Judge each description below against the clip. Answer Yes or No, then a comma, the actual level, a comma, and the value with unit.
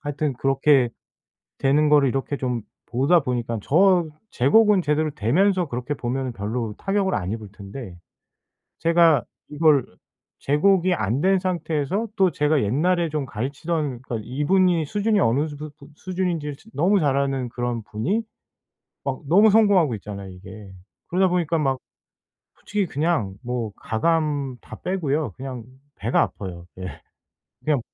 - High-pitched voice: No, medium, 145 Hz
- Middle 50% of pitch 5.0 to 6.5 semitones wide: Yes, wide, 6.0 semitones